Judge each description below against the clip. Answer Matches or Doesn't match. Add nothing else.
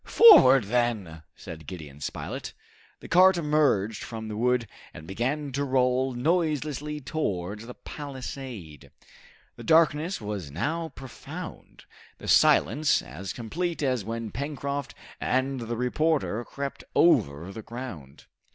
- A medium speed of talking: Doesn't match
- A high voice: Doesn't match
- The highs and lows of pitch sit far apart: Matches